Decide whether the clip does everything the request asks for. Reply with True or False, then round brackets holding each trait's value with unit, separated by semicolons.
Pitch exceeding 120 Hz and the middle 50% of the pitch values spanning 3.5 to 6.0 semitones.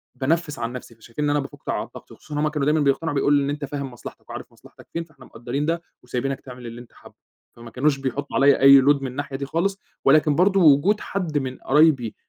False (140 Hz; 2.5 semitones)